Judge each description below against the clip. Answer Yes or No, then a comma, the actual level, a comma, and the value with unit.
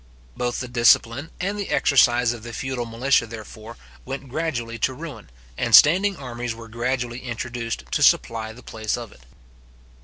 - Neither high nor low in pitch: No, low, 120 Hz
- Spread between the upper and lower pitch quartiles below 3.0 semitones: Yes, narrow, 2.4 semitones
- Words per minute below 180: Yes, average, 160 wpm